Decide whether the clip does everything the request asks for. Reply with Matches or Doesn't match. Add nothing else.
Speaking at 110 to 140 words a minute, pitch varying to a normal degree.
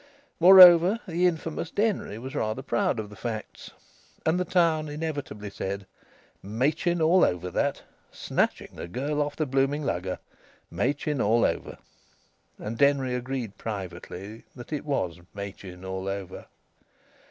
Doesn't match